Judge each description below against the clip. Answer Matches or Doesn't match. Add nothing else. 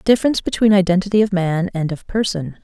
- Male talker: Doesn't match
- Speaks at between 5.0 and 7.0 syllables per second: Matches